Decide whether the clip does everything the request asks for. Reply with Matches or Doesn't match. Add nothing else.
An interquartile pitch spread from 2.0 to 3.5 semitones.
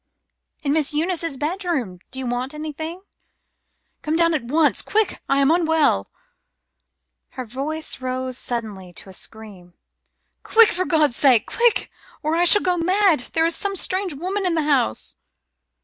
Doesn't match